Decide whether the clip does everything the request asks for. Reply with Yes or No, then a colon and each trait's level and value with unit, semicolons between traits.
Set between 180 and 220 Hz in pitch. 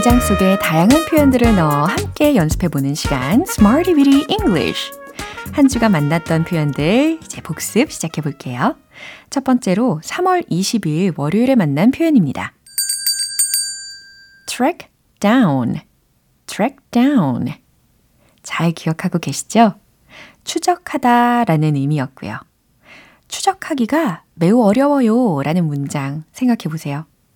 No: high, 230 Hz